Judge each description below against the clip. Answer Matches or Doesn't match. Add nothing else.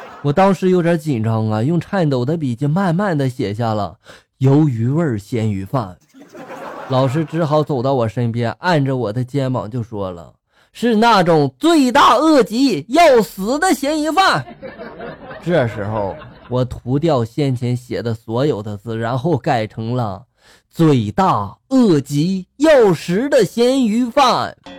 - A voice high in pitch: Doesn't match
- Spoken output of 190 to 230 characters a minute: Matches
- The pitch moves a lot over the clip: Matches